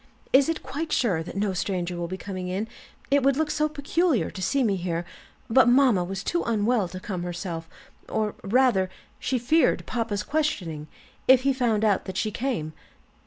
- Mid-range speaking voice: No, high, 215 Hz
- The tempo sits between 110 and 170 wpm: No, average, 185 wpm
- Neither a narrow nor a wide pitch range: No, wide, 6.3 semitones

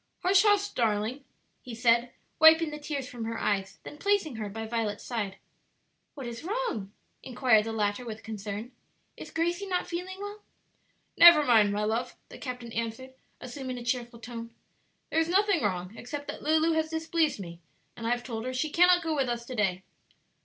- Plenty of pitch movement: Yes, wide, 6.3 semitones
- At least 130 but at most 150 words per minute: No, average, 185 wpm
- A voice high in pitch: Yes, high, 245 Hz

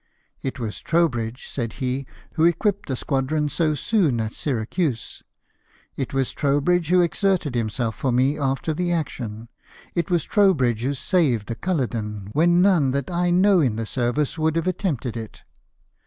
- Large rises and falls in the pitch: Yes, wide, 6.1 semitones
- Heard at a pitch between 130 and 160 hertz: Yes, medium, 140 Hz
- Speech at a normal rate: Yes, average, 170 wpm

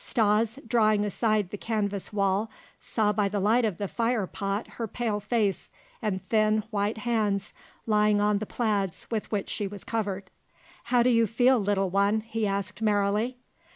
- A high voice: Yes, high, 210 Hz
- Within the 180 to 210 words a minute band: No, average, 170 wpm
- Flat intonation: Yes, narrow, 1.9 semitones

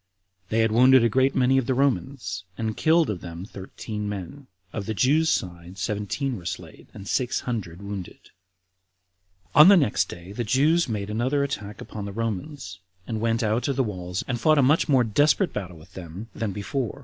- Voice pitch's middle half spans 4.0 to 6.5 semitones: Yes, average, 5.1 semitones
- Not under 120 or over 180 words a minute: No, average, 195 wpm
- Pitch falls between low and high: No, low, 115 Hz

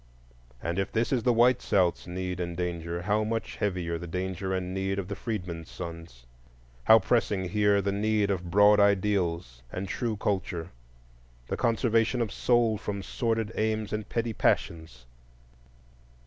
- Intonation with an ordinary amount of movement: Yes, average, 3.6 semitones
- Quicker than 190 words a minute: No, average, 155 wpm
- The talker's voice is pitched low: Yes, low, 100 Hz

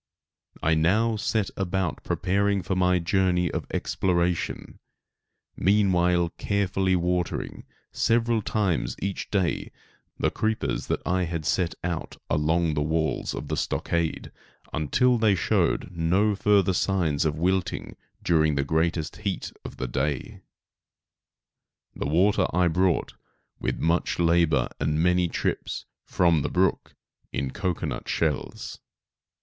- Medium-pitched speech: No, very low, 90 Hz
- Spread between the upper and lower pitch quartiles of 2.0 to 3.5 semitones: Yes, average, 2.9 semitones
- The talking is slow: Yes, slow, 125 wpm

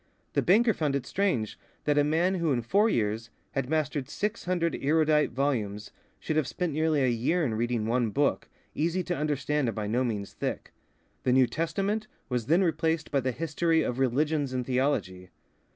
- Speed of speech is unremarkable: Yes, average, 185 wpm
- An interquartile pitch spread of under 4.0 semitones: No, average, 4.9 semitones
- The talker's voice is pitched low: No, medium, 145 Hz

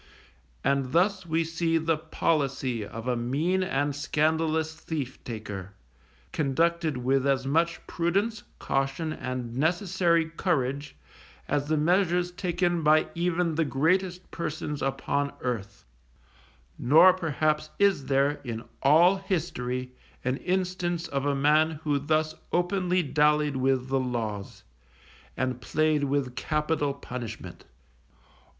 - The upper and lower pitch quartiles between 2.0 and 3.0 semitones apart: No, average, 4.0 semitones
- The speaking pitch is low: No, medium, 150 Hz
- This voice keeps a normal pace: No, slow, 120 wpm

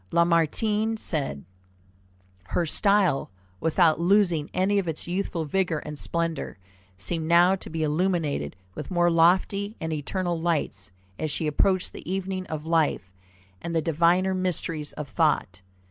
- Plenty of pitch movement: No, average, 3.0 semitones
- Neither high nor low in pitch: Yes, medium, 170 Hz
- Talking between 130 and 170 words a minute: Yes, average, 140 wpm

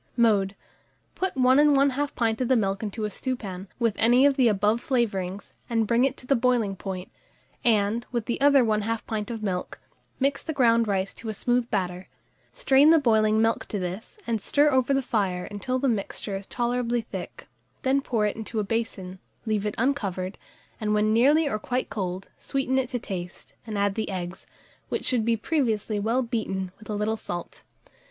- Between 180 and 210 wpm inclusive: Yes, average, 190 wpm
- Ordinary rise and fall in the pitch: Yes, average, 4.0 semitones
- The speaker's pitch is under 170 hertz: No, high, 225 Hz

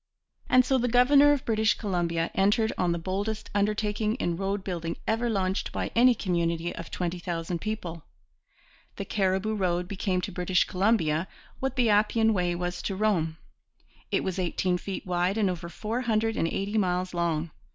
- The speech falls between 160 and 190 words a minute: Yes, average, 170 wpm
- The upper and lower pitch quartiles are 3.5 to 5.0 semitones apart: Yes, average, 3.8 semitones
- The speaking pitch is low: No, high, 190 Hz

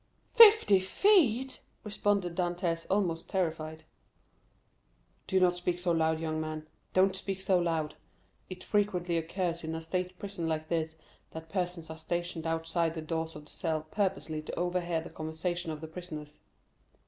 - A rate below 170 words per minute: Yes, average, 150 wpm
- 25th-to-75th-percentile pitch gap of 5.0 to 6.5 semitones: No, narrow, 2.6 semitones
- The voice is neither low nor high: Yes, medium, 170 Hz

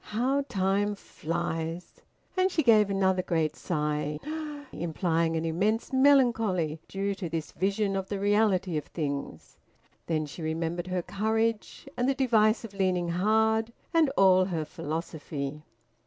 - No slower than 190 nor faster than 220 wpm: No, average, 140 wpm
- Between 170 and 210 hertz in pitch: Yes, high, 190 Hz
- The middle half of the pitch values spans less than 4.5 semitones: No, average, 4.8 semitones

